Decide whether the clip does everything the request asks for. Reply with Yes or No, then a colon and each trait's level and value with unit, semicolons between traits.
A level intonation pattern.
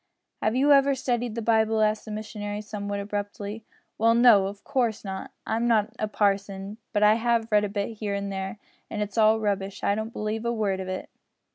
Yes: narrow, 1.9 semitones